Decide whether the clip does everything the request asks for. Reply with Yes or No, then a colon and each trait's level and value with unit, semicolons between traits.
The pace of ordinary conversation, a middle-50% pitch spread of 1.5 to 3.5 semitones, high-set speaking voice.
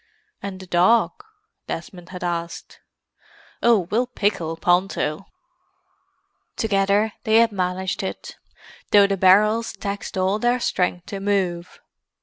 No: slow, 120 wpm; average, 2.8 semitones; high, 195 Hz